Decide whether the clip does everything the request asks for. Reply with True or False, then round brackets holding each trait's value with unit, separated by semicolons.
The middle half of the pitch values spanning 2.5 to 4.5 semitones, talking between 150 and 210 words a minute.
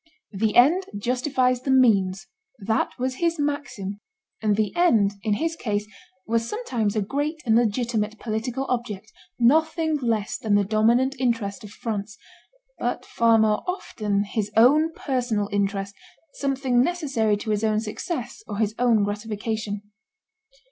False (3.8 semitones; 140 wpm)